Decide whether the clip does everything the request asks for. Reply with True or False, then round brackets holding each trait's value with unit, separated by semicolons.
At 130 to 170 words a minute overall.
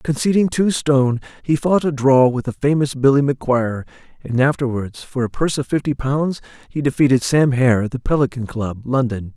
False (185 wpm)